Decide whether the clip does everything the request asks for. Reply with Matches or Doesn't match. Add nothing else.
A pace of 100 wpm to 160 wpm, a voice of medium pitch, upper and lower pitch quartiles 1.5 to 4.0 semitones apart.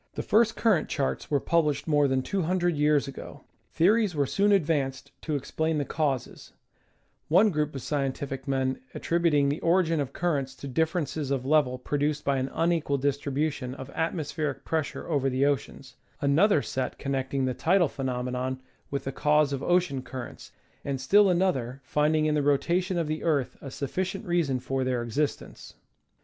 Doesn't match